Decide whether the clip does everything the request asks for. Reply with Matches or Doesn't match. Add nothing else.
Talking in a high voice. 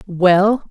Matches